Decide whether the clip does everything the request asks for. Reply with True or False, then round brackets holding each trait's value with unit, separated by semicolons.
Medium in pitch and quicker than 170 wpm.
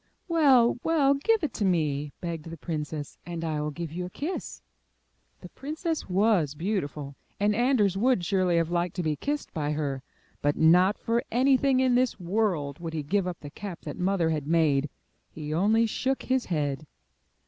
True (180 Hz; 180 wpm)